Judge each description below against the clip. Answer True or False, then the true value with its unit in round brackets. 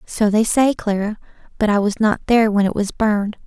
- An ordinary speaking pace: False (225 wpm)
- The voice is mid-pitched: False (210 Hz)